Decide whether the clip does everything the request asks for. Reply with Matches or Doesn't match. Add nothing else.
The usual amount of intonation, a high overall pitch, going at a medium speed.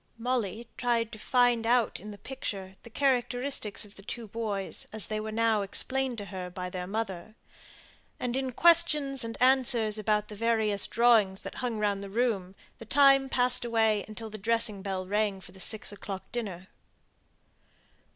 Matches